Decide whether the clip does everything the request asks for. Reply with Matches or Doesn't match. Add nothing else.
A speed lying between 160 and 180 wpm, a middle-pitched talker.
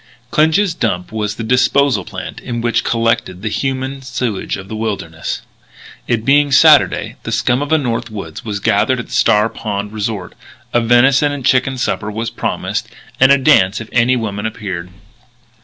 Doesn't match